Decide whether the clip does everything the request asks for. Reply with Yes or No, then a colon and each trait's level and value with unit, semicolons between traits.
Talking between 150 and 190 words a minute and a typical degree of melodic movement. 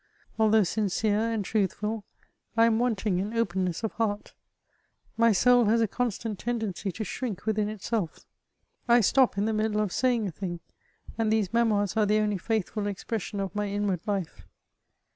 No: average, 170 wpm; narrow, 2.2 semitones